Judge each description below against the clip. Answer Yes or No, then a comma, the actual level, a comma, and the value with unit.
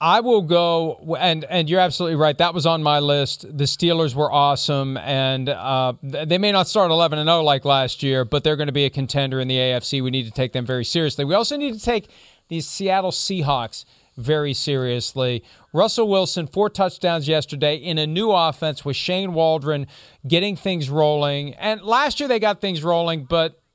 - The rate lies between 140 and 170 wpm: No, average, 200 wpm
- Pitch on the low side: No, medium, 155 Hz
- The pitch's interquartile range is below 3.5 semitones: No, average, 4.1 semitones